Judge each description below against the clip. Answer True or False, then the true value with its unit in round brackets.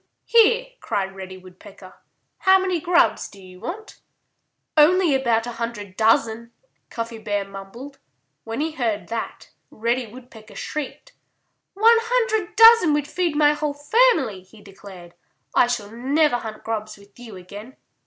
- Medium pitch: False (235 Hz)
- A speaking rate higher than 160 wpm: False (145 wpm)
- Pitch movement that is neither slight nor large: False (7.3 semitones)